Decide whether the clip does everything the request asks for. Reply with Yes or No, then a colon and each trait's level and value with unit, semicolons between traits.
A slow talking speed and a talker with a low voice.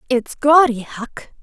No: slow, 125 wpm; very high, 260 Hz